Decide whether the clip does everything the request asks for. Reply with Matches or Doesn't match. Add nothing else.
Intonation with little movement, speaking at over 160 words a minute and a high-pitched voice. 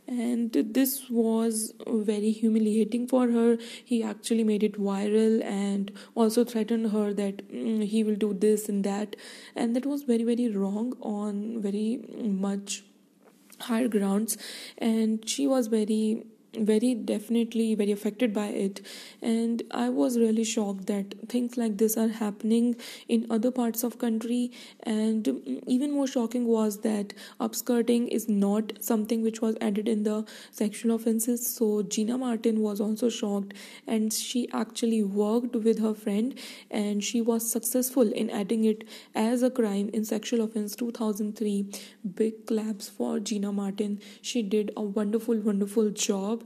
Doesn't match